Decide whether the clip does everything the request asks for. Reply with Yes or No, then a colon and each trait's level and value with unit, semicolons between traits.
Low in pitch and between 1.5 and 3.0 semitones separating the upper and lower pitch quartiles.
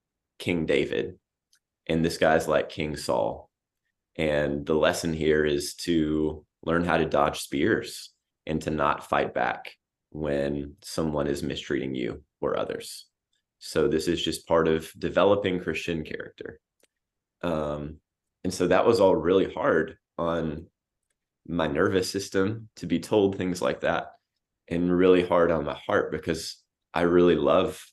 Yes: very low, 80 Hz; average, 2.7 semitones